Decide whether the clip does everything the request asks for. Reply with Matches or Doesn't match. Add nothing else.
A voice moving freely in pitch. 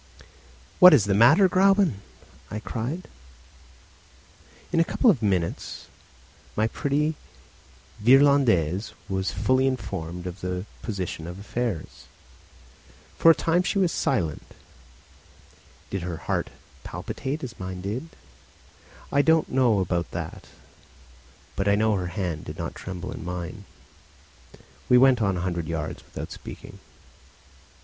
Matches